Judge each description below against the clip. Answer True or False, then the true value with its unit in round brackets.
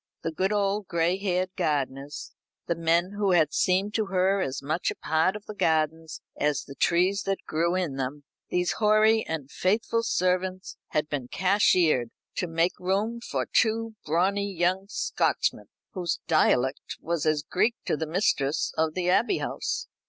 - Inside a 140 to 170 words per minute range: True (165 wpm)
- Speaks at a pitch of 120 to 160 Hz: False (180 Hz)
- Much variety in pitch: False (4.0 semitones)